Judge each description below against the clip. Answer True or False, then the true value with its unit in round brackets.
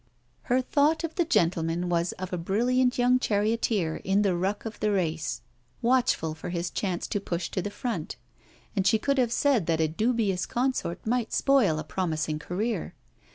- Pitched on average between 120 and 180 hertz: False (200 Hz)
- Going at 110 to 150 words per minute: False (180 wpm)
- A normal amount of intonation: False (6.1 semitones)